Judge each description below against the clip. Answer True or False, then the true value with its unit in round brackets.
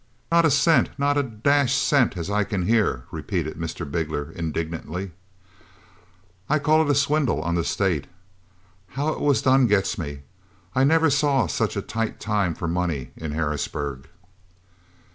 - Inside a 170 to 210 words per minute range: False (160 wpm)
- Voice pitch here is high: False (105 Hz)